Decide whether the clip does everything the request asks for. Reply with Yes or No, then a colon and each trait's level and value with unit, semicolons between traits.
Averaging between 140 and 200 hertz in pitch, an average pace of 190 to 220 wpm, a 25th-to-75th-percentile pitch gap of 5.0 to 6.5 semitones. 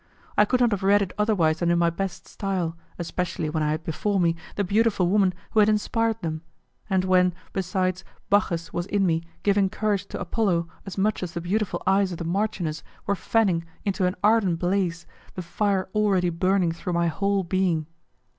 No: medium, 185 Hz; average, 195 wpm; average, 2.9 semitones